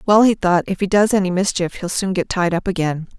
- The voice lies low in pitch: No, medium, 185 Hz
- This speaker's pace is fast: Yes, fast, 265 wpm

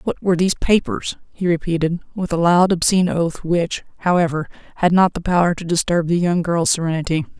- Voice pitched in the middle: Yes, medium, 170 Hz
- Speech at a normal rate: Yes, average, 185 wpm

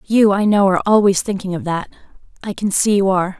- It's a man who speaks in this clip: No, female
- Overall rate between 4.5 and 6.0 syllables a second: No, 6.3 syllables/s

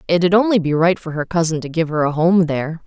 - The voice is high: No, medium, 165 Hz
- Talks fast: Yes, fast, 270 wpm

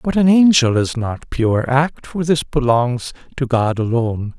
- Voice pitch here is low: Yes, low, 130 Hz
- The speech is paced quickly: No, average, 180 wpm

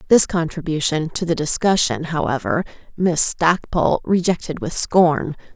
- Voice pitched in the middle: Yes, medium, 160 Hz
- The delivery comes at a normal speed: No, slow, 120 wpm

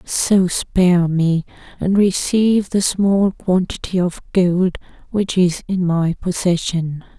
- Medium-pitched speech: Yes, medium, 180 Hz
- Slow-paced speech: Yes, slow, 125 wpm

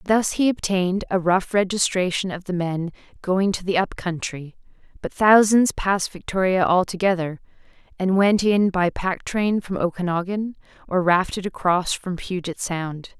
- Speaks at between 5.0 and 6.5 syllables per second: No, 4.6 syllables/s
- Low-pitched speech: No, medium, 185 Hz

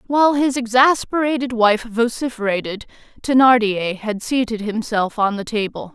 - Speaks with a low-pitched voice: No, high, 230 Hz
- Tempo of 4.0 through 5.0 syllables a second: Yes, 4.8 syllables/s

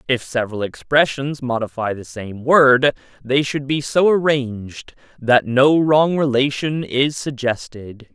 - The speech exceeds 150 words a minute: No, slow, 135 wpm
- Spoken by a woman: No, male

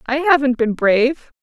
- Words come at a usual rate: Yes, average, 170 wpm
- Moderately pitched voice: No, very high, 265 Hz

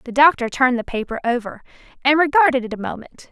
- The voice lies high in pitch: Yes, very high, 260 Hz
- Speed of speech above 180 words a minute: Yes, average, 200 wpm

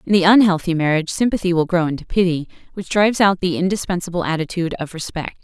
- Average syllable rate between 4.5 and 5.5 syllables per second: No, 6.8 syllables/s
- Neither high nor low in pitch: Yes, medium, 175 Hz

